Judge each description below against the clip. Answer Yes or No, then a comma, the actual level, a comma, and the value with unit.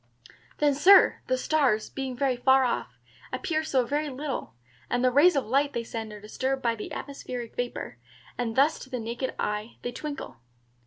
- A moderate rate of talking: Yes, average, 180 wpm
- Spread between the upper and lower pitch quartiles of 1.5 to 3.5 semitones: Yes, average, 3.1 semitones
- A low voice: No, very high, 260 Hz